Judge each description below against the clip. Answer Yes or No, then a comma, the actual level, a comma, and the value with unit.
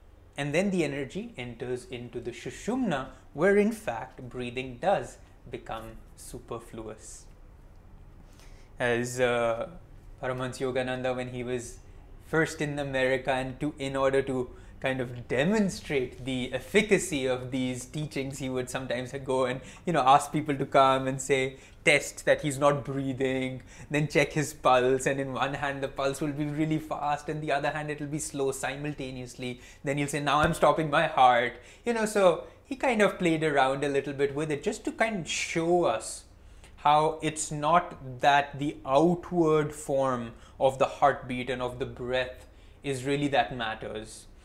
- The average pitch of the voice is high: No, low, 135 Hz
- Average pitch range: Yes, average, 3.3 semitones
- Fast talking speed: No, average, 165 wpm